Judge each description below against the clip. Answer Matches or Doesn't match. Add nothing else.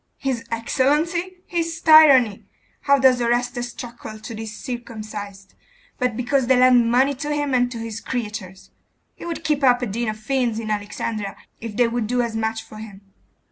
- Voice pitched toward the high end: Matches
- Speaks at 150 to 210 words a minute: Matches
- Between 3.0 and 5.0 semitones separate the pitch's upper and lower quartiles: Matches